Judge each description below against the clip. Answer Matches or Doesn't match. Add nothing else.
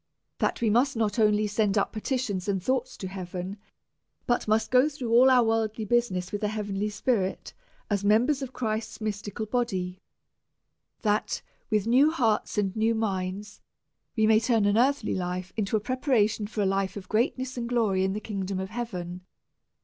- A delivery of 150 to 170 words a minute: Doesn't match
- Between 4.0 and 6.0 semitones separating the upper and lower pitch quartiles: Doesn't match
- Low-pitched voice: Doesn't match